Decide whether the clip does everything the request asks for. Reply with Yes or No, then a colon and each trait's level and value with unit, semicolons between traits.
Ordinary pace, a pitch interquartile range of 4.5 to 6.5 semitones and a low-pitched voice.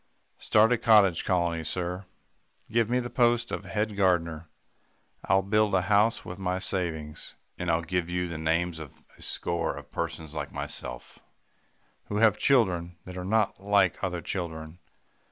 No: average, 160 wpm; average, 3.7 semitones; very low, 90 Hz